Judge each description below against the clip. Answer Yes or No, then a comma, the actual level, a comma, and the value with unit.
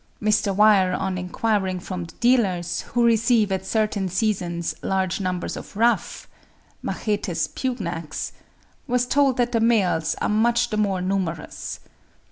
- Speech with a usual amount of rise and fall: Yes, average, 4.0 semitones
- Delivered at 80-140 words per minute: Yes, slow, 135 wpm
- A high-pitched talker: Yes, high, 200 Hz